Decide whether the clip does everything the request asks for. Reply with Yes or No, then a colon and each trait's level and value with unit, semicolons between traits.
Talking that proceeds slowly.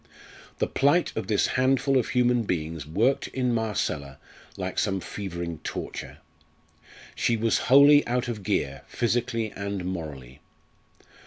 Yes: slow, 130 wpm